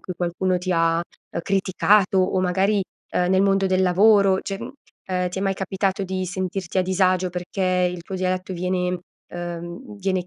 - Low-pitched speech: No, medium, 185 Hz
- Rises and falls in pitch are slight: Yes, narrow, 1.2 semitones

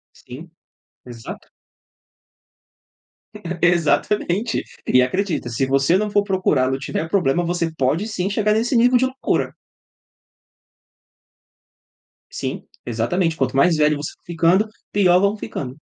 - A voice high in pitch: No, medium, 175 Hz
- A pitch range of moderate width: No, wide, 5.9 semitones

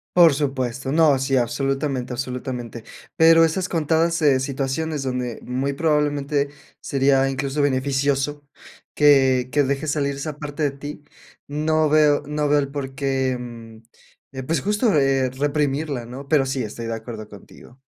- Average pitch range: No, narrow, 2.2 semitones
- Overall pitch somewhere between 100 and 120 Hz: No, medium, 140 Hz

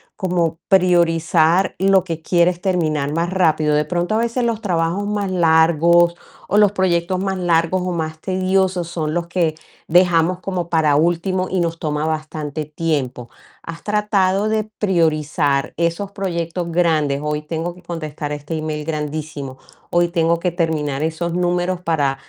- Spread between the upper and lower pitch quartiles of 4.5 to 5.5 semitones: No, average, 2.7 semitones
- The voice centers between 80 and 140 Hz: No, medium, 170 Hz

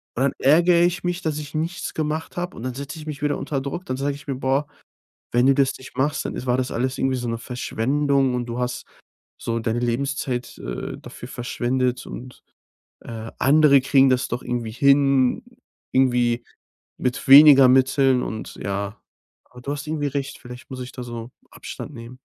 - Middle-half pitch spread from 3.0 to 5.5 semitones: No, narrow, 2.6 semitones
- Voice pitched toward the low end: Yes, low, 130 Hz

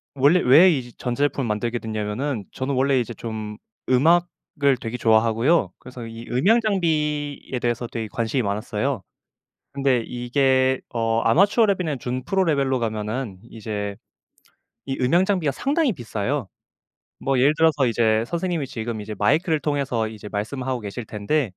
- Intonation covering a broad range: No, average, 4.7 semitones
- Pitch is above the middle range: No, low, 125 Hz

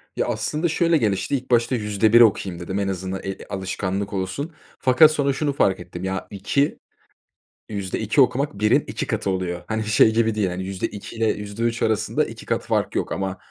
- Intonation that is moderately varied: Yes, average, 4.1 semitones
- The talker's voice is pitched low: Yes, low, 105 Hz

